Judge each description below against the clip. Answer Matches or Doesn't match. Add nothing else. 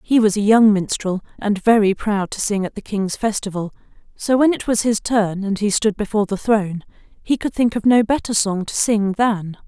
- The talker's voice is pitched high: Matches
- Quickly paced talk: Matches